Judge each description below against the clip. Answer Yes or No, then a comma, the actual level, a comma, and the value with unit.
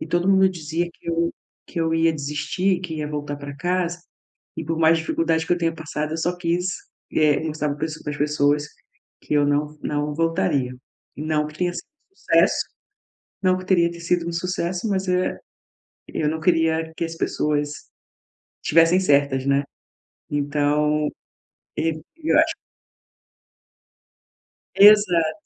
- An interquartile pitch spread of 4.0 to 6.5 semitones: No, average, 2.7 semitones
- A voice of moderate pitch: Yes, medium, 160 Hz